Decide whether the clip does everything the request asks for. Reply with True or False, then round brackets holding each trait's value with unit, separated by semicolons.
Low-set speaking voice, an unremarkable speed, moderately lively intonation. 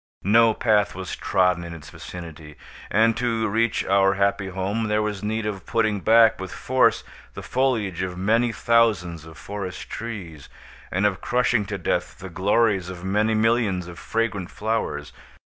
True (100 Hz; 165 wpm; 3.5 semitones)